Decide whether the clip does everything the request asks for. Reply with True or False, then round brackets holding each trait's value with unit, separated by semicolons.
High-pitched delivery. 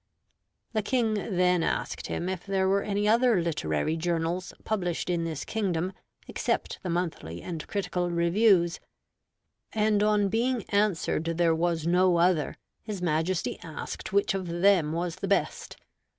False (180 Hz)